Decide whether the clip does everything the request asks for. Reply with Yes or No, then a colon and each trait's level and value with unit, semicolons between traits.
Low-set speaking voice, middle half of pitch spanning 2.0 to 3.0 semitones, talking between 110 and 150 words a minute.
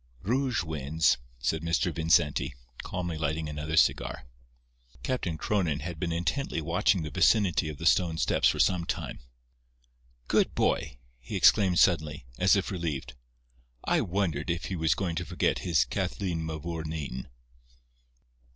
Yes: very low, 85 Hz; average, 2.7 semitones; average, 140 wpm